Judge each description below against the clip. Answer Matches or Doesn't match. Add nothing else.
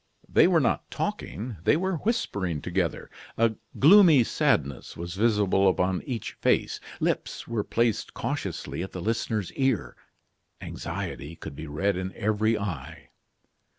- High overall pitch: Doesn't match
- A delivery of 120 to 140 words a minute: Matches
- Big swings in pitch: Doesn't match